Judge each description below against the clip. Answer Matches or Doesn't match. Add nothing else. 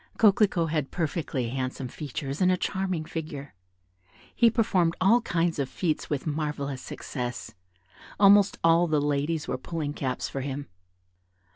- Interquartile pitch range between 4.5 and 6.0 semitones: Doesn't match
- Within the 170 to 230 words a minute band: Doesn't match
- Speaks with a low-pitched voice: Doesn't match